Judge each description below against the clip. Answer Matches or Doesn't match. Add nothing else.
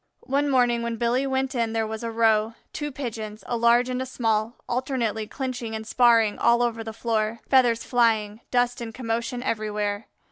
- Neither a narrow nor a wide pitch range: Doesn't match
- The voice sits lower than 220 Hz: Doesn't match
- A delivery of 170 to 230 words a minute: Matches